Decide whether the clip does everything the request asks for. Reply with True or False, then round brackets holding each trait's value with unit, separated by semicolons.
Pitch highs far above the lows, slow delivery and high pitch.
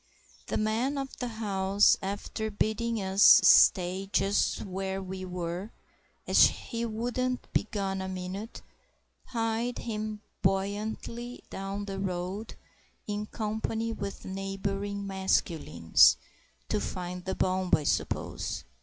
False (2.5 semitones; 115 wpm; 200 Hz)